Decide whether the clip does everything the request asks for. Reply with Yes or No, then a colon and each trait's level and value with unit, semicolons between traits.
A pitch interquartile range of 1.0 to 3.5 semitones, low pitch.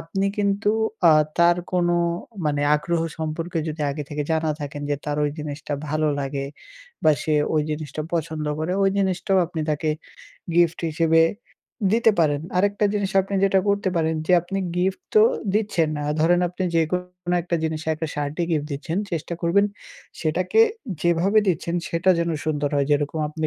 No: average, 2.9 semitones; medium, 165 Hz